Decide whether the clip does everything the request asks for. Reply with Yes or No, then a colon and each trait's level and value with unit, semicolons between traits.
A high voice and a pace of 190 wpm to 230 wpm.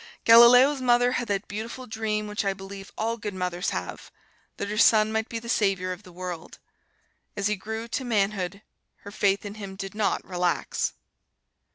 No: high, 210 Hz; average, 180 wpm